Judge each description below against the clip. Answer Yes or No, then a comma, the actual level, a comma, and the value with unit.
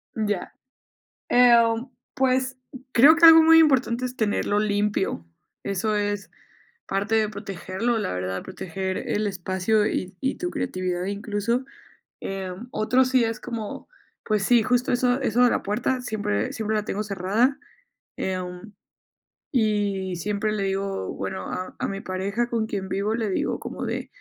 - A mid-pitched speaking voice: No, high, 210 Hz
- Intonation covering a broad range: No, average, 3.8 semitones